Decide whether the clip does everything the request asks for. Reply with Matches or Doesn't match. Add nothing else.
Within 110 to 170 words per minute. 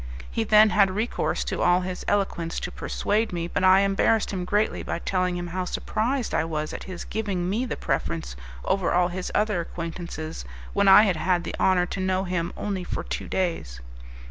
Doesn't match